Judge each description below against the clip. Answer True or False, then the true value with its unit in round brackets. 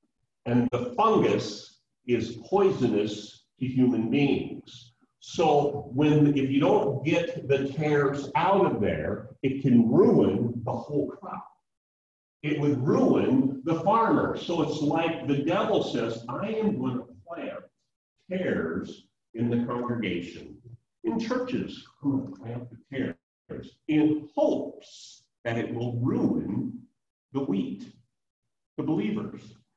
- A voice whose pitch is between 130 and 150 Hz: True (135 Hz)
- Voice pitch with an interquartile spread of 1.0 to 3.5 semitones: False (3.9 semitones)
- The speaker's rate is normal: False (120 wpm)